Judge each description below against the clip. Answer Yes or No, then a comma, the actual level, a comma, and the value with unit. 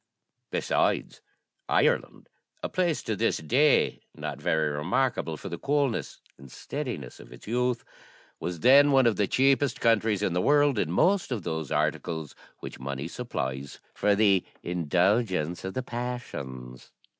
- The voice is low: Yes, low, 105 Hz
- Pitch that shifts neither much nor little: No, wide, 8.2 semitones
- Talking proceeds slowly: No, average, 145 wpm